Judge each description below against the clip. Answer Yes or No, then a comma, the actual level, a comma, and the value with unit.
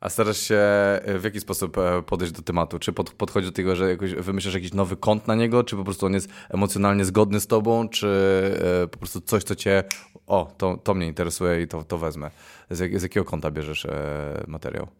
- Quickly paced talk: Yes, fast, 200 wpm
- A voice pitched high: No, very low, 95 Hz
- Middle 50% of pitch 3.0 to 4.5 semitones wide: No, narrow, 2.4 semitones